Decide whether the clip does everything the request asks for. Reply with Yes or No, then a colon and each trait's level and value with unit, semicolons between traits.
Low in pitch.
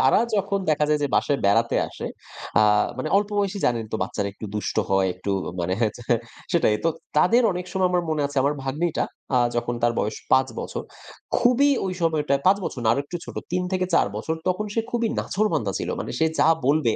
No: medium, 150 Hz